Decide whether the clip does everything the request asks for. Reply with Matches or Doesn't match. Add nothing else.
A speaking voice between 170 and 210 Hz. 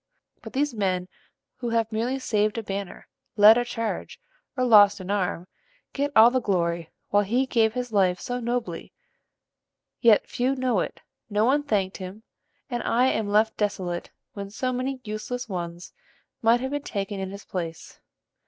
Doesn't match